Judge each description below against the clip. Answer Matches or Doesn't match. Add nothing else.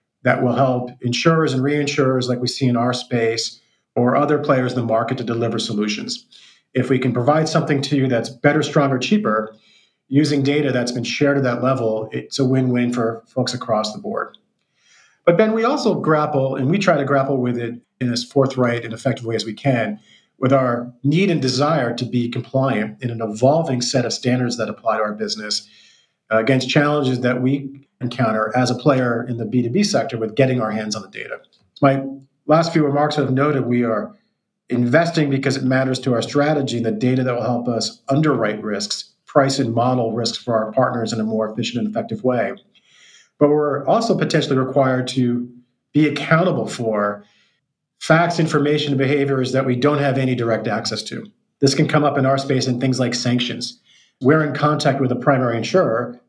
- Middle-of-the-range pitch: Doesn't match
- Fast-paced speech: Doesn't match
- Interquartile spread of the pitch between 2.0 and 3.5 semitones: Matches